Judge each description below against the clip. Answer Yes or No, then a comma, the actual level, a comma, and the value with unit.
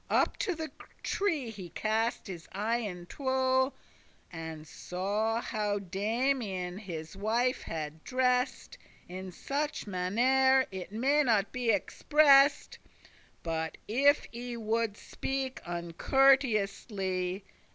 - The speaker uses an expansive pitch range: Yes, wide, 5.9 semitones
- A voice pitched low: No, high, 220 Hz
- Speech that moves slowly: Yes, slow, 105 wpm